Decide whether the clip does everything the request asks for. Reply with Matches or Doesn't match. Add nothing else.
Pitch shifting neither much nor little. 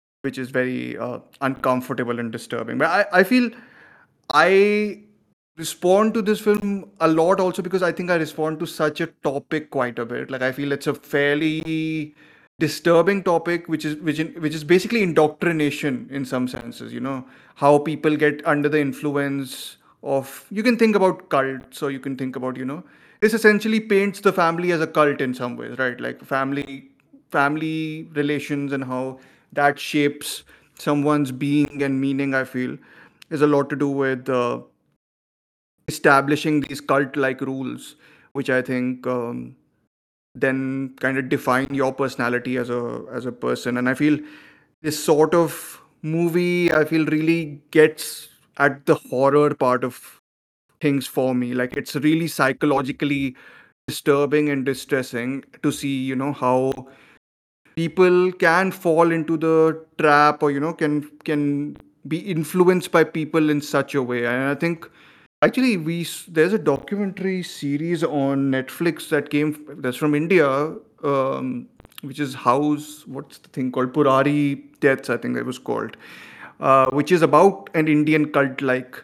Matches